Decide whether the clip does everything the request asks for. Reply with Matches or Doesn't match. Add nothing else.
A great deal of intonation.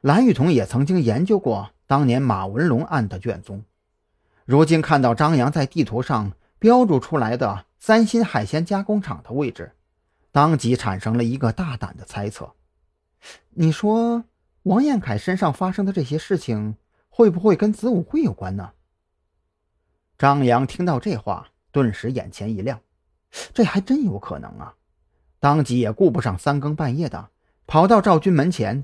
Matches